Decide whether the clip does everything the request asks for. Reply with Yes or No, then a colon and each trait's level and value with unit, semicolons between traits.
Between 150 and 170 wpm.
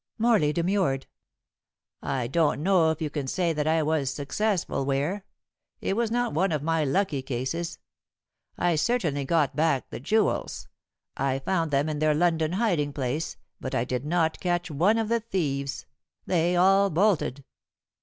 Yes: average, 160 wpm